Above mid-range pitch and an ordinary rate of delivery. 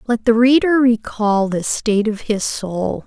Yes: high, 225 Hz; average, 175 wpm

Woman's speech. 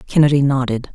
Yes: female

